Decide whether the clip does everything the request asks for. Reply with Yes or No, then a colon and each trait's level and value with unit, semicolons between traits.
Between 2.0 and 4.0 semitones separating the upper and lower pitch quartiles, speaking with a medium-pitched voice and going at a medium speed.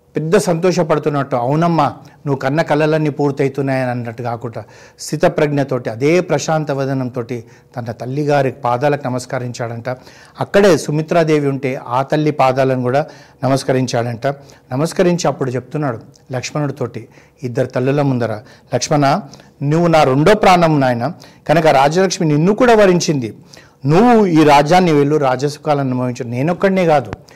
Yes: average, 3.4 semitones; medium, 145 Hz; average, 110 wpm